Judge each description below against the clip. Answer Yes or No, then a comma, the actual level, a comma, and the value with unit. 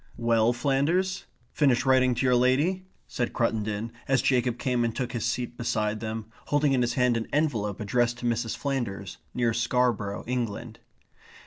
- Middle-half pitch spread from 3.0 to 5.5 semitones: No, narrow, 2.4 semitones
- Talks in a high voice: No, low, 120 Hz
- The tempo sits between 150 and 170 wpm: Yes, average, 160 wpm